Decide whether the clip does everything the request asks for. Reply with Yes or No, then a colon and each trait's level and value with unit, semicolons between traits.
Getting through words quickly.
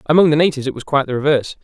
Yes: fast, 295 wpm